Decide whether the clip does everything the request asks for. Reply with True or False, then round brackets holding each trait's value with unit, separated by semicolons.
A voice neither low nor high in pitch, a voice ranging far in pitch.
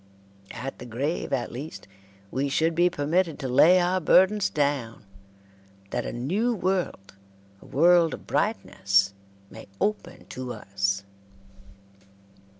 True (145 Hz; 6.5 semitones)